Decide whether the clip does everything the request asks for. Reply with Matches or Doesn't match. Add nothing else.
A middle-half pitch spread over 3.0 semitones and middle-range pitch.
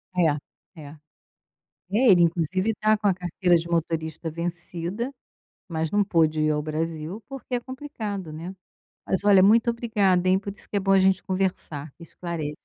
Matches